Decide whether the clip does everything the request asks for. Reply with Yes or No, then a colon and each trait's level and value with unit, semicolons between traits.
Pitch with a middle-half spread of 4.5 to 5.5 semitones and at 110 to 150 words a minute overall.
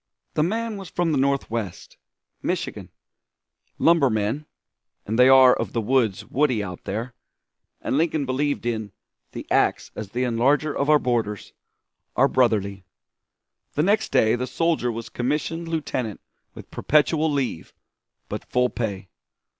Yes: average, 5.1 semitones; average, 140 wpm